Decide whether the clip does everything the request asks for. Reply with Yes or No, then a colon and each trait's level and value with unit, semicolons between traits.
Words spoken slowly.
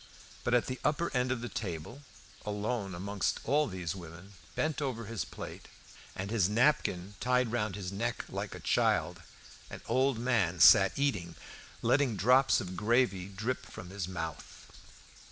No: average, 160 wpm